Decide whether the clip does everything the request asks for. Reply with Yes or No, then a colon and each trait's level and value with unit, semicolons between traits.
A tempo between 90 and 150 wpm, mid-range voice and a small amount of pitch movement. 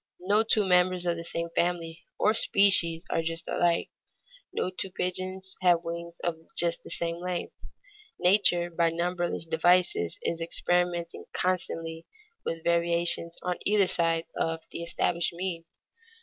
Yes: average, 140 wpm; medium, 170 Hz; narrow, 1.4 semitones